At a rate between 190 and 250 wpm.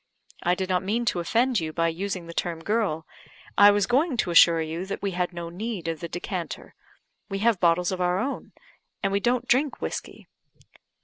Yes: average, 200 wpm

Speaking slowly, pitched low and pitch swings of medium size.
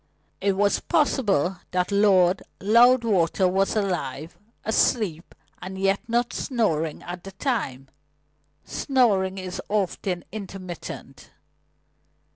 No: slow, 95 wpm; high, 195 Hz; average, 3.3 semitones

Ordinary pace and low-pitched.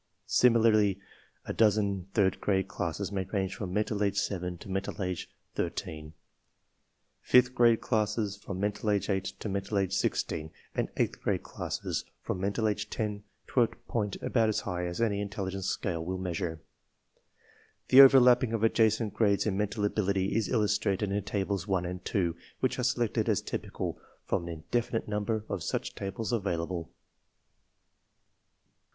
Yes: average, 160 wpm; low, 100 Hz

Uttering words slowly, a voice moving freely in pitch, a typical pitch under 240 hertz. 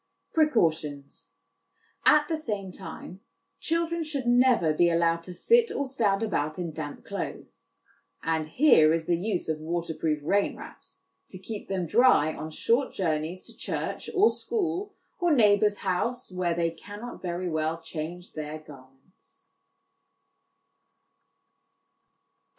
Yes: slow, 130 wpm; wide, 8.0 semitones; medium, 185 Hz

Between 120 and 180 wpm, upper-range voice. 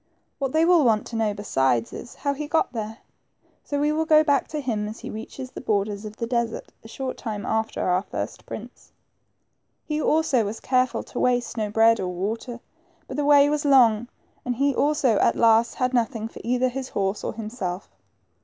No: fast, 205 wpm; high, 235 Hz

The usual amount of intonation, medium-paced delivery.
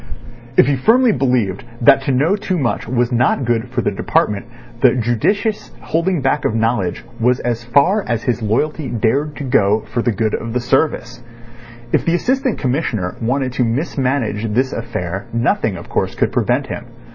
Yes: average, 3.7 semitones; average, 180 wpm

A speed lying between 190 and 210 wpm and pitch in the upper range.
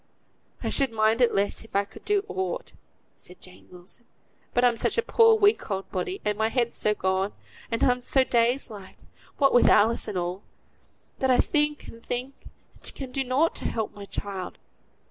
Yes: average, 195 wpm; high, 235 Hz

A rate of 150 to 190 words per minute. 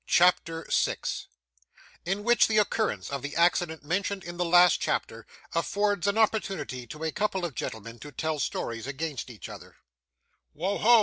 Yes: average, 165 wpm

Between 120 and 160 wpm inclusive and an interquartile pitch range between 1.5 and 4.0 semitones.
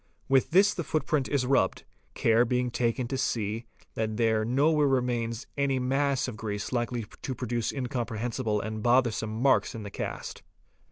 Yes: average, 155 wpm; average, 2.9 semitones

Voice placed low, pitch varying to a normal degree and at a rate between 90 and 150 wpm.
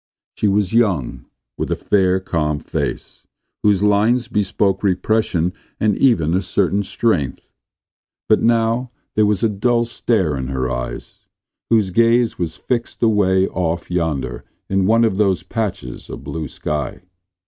Yes: very low, 95 Hz; average, 4.8 semitones; average, 145 wpm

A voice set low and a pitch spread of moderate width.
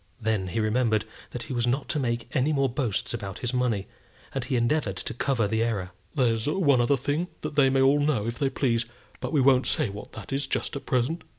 Yes: low, 125 Hz; average, 3.5 semitones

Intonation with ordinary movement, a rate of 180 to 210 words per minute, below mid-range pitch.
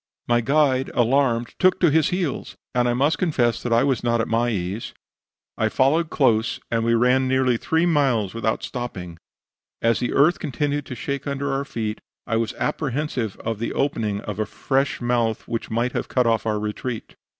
Yes: average, 3.5 semitones; average, 190 wpm; low, 125 Hz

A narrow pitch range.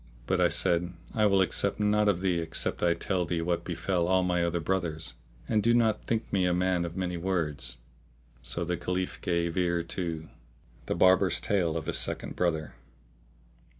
Yes: narrow, 2.0 semitones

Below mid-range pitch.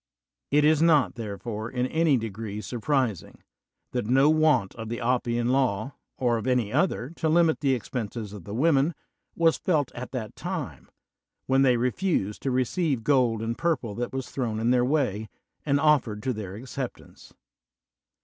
Yes: low, 125 Hz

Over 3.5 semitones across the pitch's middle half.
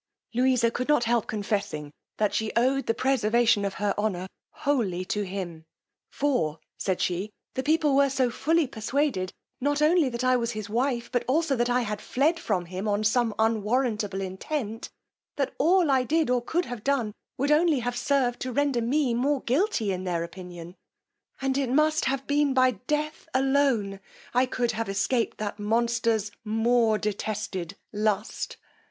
Yes: average, 4.7 semitones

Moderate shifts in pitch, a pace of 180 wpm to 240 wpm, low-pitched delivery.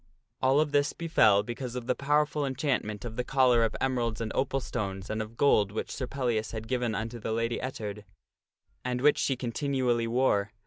Yes: average, 3.2 semitones; average, 190 wpm; low, 120 Hz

